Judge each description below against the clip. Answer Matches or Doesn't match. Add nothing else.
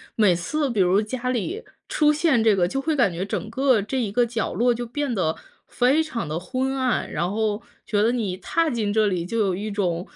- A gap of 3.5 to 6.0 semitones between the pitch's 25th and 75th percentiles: Matches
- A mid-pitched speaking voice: Doesn't match